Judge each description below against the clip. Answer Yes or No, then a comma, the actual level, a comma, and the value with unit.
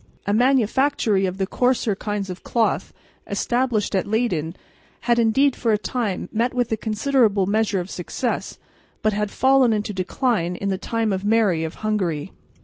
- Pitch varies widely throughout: No, average, 3.7 semitones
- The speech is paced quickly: No, average, 165 wpm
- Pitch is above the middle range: Yes, high, 215 Hz